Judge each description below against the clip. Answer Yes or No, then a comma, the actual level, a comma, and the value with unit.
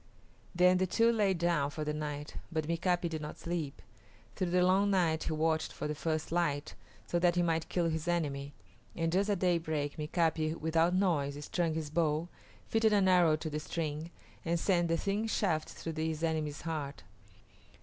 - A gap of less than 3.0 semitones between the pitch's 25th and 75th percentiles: Yes, narrow, 2.4 semitones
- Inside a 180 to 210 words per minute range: Yes, average, 185 wpm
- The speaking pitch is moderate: Yes, medium, 165 Hz